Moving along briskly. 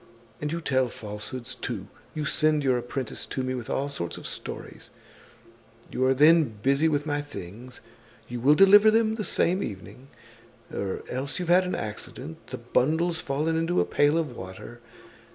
No: average, 170 wpm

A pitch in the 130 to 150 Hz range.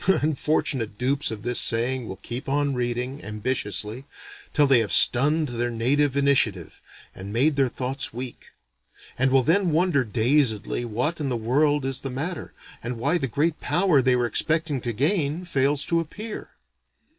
Yes: low, 135 Hz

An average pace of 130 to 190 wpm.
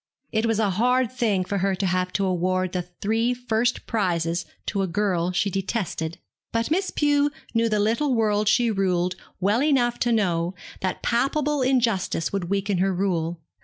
Yes: average, 175 wpm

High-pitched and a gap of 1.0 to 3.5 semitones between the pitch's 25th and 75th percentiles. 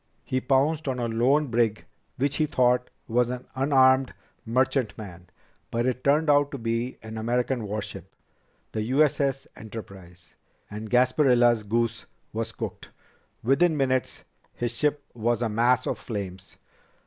No: low, 120 Hz; average, 3.1 semitones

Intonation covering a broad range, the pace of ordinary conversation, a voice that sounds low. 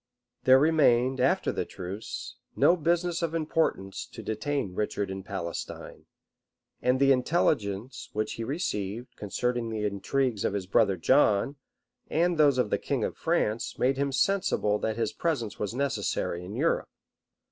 Yes: wide, 5.7 semitones; average, 150 wpm; low, 125 Hz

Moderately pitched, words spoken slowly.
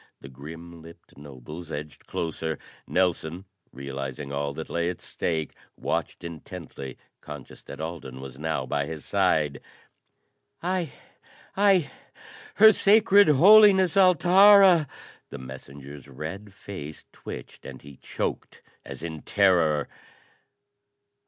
No: very low, 80 Hz; slow, 115 wpm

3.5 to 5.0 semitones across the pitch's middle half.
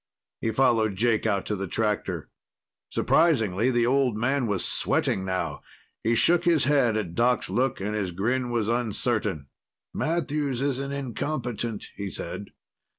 Yes: average, 4.4 semitones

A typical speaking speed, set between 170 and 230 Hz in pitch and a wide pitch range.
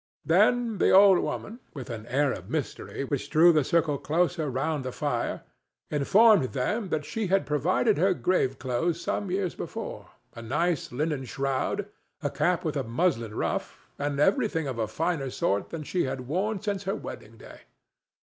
No: average, 170 wpm; medium, 155 Hz; wide, 5.9 semitones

